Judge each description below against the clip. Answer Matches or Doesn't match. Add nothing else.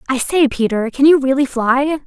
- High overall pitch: Matches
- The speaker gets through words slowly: Doesn't match